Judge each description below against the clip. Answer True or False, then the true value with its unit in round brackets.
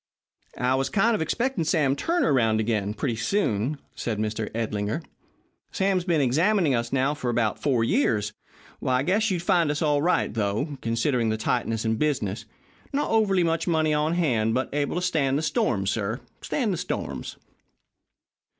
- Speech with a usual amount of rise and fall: False (7.0 semitones)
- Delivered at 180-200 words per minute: False (170 wpm)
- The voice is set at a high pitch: False (140 Hz)